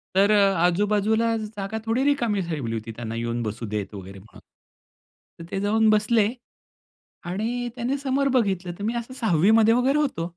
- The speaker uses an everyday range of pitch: No, wide, 5.8 semitones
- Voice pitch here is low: No, high, 210 Hz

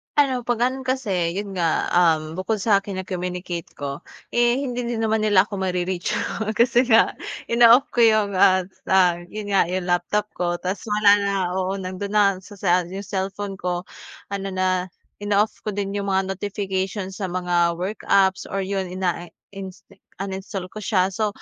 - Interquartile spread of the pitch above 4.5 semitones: No, narrow, 2.4 semitones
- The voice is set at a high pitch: Yes, high, 195 Hz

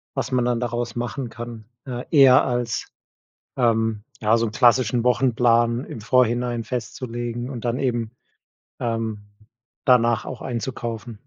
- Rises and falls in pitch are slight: Yes, narrow, 1.4 semitones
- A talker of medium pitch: No, low, 120 Hz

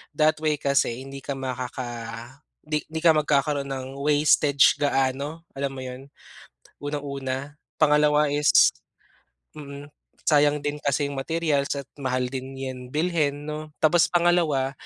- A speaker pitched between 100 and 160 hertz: Yes, medium, 140 Hz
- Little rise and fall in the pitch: Yes, narrow, 2.1 semitones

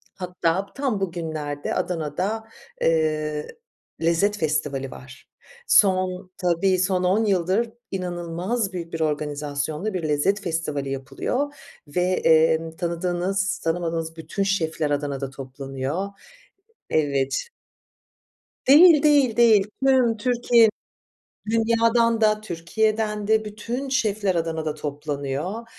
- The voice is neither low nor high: Yes, medium, 180 Hz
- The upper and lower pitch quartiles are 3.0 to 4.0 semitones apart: No, wide, 5.6 semitones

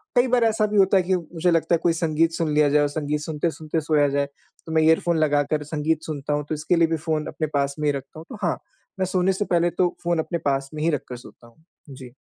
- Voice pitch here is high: No, medium, 160 Hz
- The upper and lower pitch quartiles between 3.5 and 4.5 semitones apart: No, narrow, 2.6 semitones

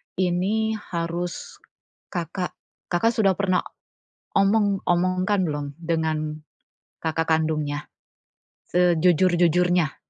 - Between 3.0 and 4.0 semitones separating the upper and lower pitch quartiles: No, narrow, 2.6 semitones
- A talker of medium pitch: Yes, medium, 175 Hz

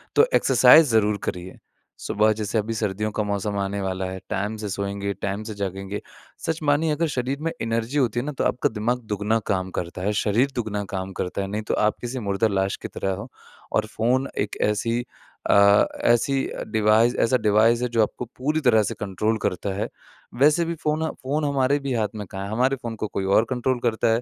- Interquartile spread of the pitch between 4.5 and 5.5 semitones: No, average, 3.7 semitones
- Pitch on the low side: Yes, low, 110 Hz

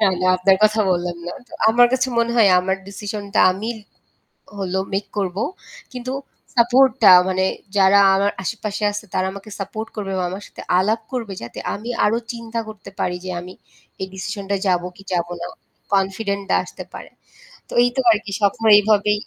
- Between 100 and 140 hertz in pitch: No, high, 200 Hz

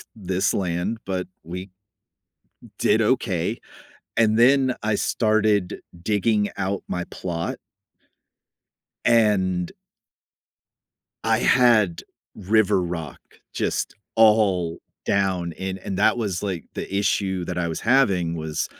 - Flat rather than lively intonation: No, average, 3.4 semitones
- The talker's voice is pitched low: Yes, very low, 95 Hz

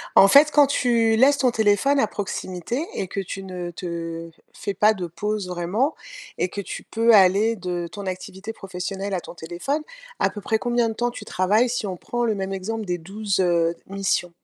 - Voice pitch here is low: No, high, 200 Hz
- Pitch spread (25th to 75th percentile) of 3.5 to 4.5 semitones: Yes, average, 3.8 semitones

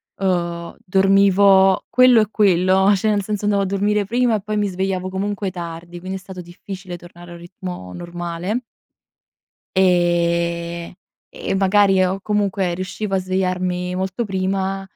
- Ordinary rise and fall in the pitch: No, narrow, 2.1 semitones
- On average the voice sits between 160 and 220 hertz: Yes, high, 190 Hz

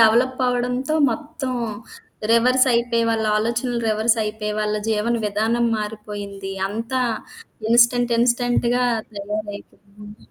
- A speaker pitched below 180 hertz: No, high, 230 Hz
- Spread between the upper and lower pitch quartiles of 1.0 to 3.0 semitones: Yes, narrow, 2.5 semitones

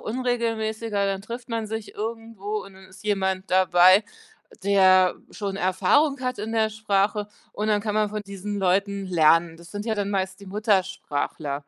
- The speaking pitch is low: No, high, 200 Hz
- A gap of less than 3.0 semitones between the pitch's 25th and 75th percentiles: Yes, narrow, 2.5 semitones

